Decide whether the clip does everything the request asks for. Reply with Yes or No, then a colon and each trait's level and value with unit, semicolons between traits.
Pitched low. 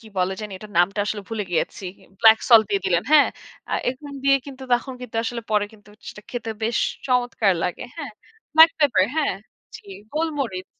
No: high, 225 Hz